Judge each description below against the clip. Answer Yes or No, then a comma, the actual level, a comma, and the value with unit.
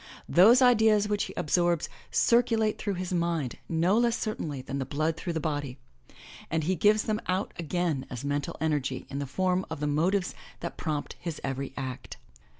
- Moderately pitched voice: Yes, medium, 170 Hz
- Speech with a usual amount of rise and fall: No, wide, 5.8 semitones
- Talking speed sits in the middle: Yes, average, 175 wpm